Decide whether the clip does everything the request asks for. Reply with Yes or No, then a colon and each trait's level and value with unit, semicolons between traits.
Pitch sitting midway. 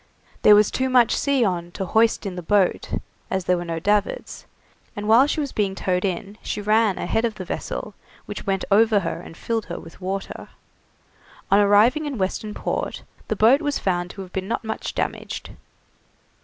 No: high, 205 Hz